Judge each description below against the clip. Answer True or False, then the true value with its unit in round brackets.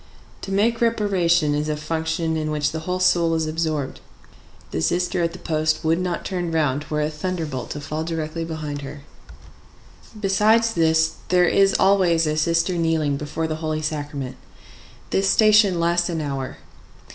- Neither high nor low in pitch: True (160 Hz)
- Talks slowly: False (165 wpm)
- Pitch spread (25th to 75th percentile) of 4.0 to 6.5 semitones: False (2.7 semitones)